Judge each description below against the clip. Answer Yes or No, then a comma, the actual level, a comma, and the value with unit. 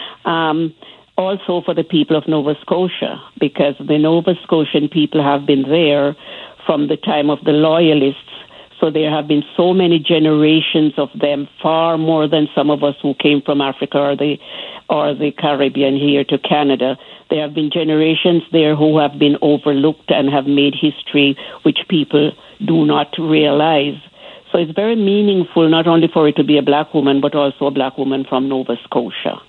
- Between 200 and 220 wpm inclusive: No, average, 180 wpm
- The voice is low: No, medium, 150 Hz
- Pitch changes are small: Yes, narrow, 2.2 semitones